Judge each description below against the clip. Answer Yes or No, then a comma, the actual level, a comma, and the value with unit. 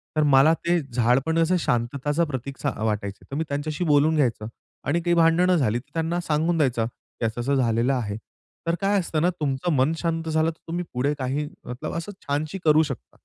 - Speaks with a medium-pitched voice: Yes, medium, 150 Hz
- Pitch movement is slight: No, average, 4.3 semitones